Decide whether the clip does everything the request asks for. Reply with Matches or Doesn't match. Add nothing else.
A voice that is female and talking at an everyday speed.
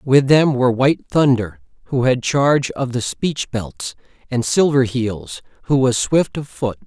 Doesn't match